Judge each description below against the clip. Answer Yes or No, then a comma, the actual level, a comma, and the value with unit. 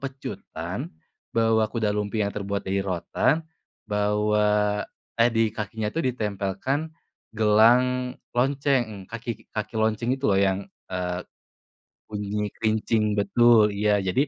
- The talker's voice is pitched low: Yes, low, 110 Hz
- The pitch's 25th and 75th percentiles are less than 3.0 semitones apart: Yes, narrow, 2.5 semitones